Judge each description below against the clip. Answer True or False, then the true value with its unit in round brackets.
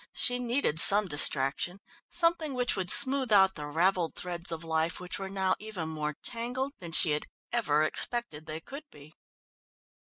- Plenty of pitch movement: True (7.1 semitones)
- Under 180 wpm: True (165 wpm)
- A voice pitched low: False (185 Hz)